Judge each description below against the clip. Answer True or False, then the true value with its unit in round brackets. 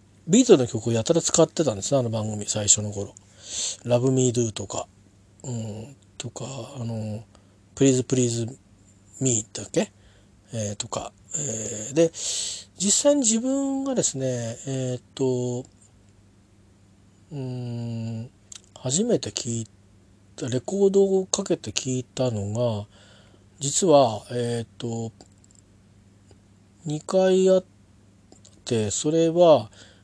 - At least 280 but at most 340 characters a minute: False (215 characters per minute)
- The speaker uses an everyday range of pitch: True (4.8 semitones)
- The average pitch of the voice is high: False (115 Hz)